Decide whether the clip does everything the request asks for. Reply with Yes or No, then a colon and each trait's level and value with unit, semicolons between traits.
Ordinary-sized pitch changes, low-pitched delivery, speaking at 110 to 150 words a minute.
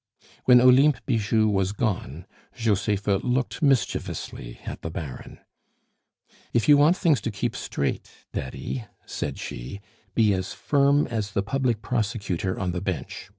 Yes: average, 5.0 semitones; low, 110 Hz; average, 140 wpm